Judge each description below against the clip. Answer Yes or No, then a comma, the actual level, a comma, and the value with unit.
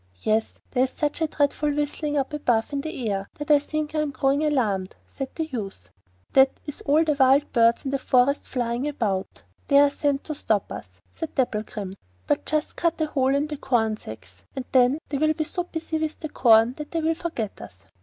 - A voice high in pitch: Yes, very high, 275 Hz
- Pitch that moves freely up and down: No, average, 4.8 semitones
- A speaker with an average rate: No, fast, 215 wpm